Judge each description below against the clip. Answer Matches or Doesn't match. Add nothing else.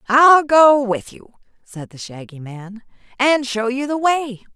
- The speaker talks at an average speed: Matches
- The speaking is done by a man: Doesn't match